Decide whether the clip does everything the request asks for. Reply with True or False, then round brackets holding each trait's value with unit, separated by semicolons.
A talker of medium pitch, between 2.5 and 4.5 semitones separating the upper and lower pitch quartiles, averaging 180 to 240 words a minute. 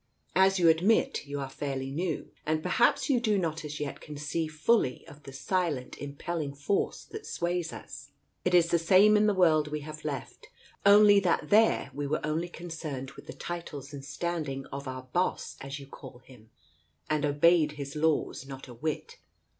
True (155 Hz; 3.9 semitones; 185 wpm)